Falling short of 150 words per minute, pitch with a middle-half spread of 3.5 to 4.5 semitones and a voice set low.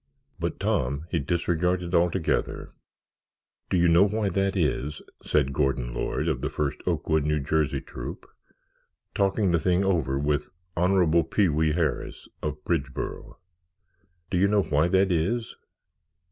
Yes: average, 140 wpm; average, 3.9 semitones; very low, 85 Hz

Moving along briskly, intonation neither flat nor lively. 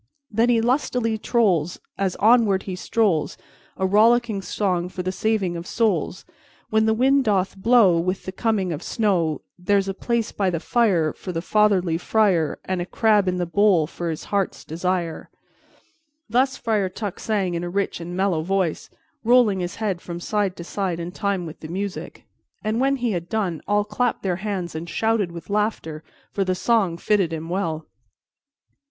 No: average, 180 wpm; average, 3.8 semitones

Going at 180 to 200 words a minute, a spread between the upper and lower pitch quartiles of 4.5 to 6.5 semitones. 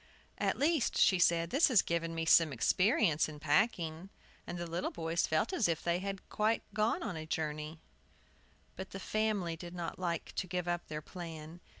No: average, 185 wpm; average, 3.2 semitones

